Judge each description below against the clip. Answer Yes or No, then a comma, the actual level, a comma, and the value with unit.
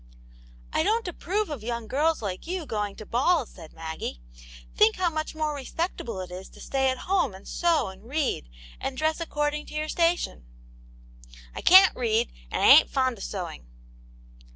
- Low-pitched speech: No, very high, 265 Hz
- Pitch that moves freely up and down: Yes, wide, 7.7 semitones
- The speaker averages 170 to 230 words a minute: Yes, average, 190 wpm